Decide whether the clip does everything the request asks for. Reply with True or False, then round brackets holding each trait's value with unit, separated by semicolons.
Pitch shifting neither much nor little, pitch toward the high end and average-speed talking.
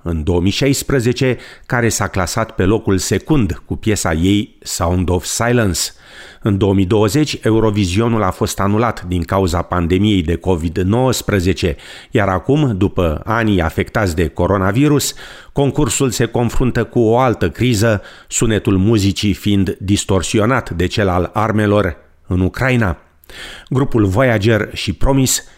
False (4.1 semitones; 105 Hz; 125 wpm)